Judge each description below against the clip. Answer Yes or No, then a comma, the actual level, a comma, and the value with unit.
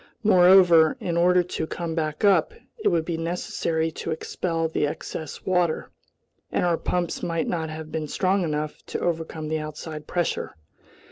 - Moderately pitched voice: Yes, medium, 165 Hz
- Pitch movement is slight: Yes, narrow, 1.9 semitones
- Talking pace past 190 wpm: No, average, 160 wpm